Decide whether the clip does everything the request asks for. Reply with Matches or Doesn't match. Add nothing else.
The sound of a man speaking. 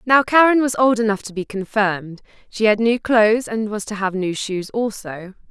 Doesn't match